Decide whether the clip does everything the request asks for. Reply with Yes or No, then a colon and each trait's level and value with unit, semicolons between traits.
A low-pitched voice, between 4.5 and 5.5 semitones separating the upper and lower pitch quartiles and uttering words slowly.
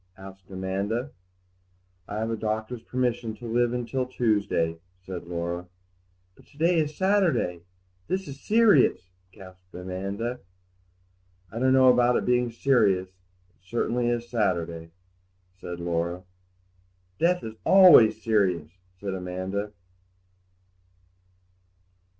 Yes: low, 105 Hz; average, 5.1 semitones; slow, 115 wpm